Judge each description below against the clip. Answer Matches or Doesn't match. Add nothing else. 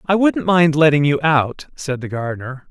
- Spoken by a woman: Doesn't match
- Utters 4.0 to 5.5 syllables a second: Matches